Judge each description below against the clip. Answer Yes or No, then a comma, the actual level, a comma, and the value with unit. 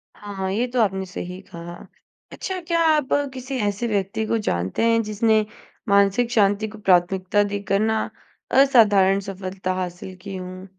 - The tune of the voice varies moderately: Yes, average, 3.0 semitones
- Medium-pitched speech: No, high, 200 Hz